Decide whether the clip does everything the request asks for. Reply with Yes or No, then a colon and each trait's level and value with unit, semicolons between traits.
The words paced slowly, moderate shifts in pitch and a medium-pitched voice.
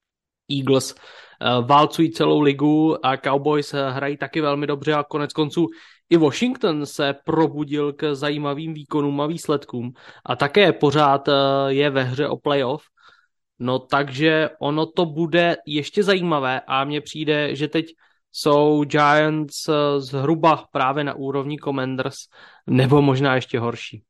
No: slow, 130 wpm; narrow, 1.9 semitones; medium, 145 Hz